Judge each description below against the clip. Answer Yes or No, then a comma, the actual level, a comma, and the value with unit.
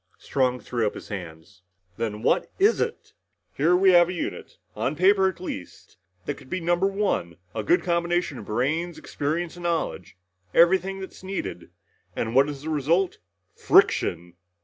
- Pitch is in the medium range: Yes, medium, 165 Hz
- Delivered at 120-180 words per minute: Yes, average, 165 wpm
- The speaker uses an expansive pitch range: Yes, wide, 7.6 semitones